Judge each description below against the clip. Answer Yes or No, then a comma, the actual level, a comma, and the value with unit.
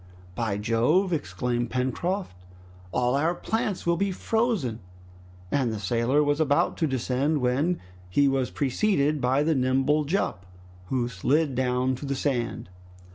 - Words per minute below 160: Yes, average, 140 wpm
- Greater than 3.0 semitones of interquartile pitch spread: Yes, average, 4.2 semitones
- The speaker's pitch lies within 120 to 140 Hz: Yes, low, 135 Hz